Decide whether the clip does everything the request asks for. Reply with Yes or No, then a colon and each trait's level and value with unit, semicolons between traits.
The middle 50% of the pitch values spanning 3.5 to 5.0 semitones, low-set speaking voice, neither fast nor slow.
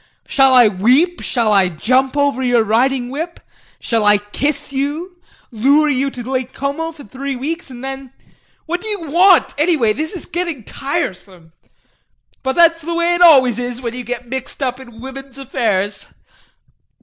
No: average, 4.3 semitones; very high, 265 Hz; average, 170 wpm